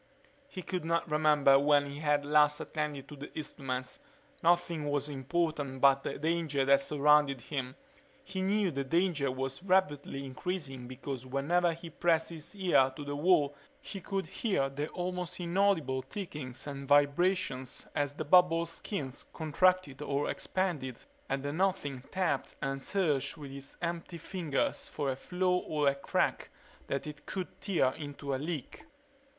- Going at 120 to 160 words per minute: Yes, average, 155 wpm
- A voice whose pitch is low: No, medium, 150 Hz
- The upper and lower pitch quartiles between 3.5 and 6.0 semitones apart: Yes, average, 4.1 semitones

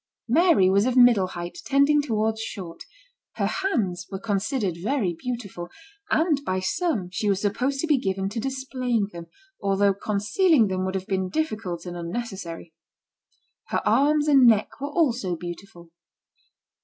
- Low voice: No, high, 210 Hz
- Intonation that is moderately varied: No, wide, 6.2 semitones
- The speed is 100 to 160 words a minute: Yes, average, 150 wpm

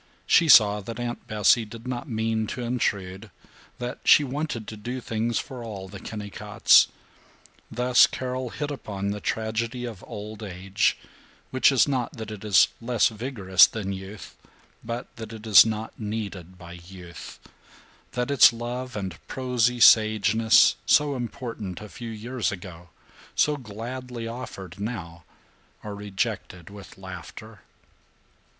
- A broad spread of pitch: No, average, 3.4 semitones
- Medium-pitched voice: No, low, 110 Hz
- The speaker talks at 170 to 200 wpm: No, average, 140 wpm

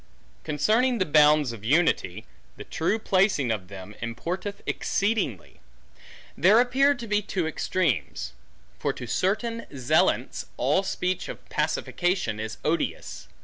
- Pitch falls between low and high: Yes, medium, 170 Hz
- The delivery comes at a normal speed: No, slow, 125 wpm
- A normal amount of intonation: No, wide, 8.9 semitones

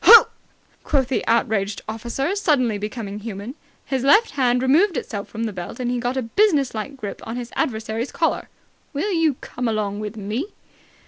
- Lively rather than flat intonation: No, average, 4.2 semitones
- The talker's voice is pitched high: Yes, high, 245 Hz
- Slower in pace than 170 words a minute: No, average, 175 wpm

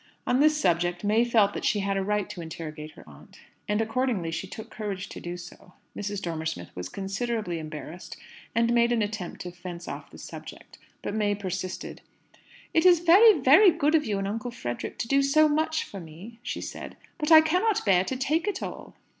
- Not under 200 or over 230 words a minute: Yes, fast, 205 wpm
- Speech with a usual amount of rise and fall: No, wide, 7.2 semitones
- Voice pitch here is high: Yes, high, 210 Hz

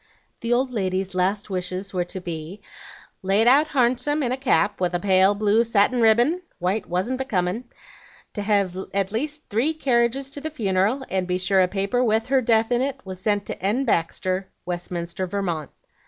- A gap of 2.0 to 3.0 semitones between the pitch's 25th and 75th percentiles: No, average, 4.9 semitones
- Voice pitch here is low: No, high, 205 Hz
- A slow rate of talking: No, average, 185 wpm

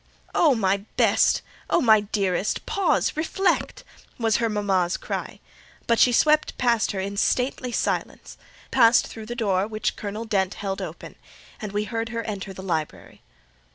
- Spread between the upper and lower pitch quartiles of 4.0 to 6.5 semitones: No, average, 3.3 semitones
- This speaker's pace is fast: No, average, 155 wpm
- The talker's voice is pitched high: Yes, high, 215 Hz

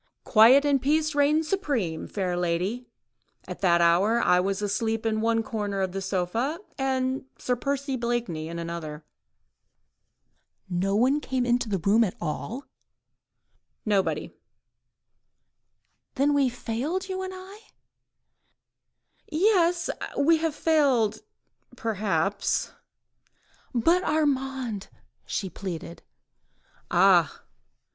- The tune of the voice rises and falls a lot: Yes, wide, 6.6 semitones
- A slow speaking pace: Yes, slow, 110 wpm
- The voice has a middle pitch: No, high, 230 Hz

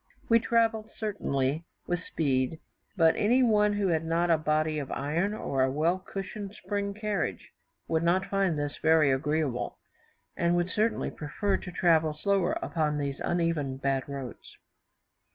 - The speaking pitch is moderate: Yes, medium, 165 Hz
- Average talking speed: Yes, average, 155 wpm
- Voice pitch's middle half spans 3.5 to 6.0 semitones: Yes, average, 5.1 semitones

